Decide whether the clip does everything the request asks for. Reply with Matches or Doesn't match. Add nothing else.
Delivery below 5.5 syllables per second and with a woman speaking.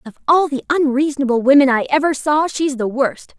Doesn't match